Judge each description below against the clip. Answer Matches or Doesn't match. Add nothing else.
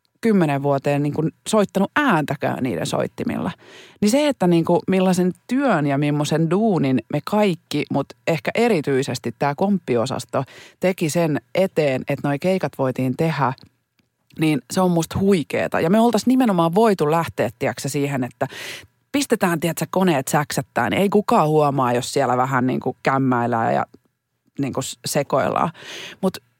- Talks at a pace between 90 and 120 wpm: Doesn't match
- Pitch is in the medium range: Matches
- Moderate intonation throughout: Doesn't match